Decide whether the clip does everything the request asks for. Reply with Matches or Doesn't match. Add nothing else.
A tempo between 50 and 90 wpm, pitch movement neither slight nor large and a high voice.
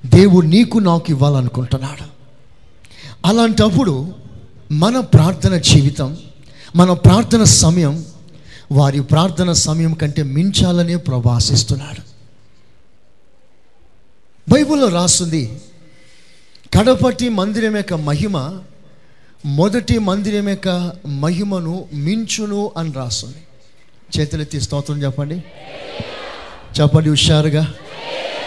Doesn't match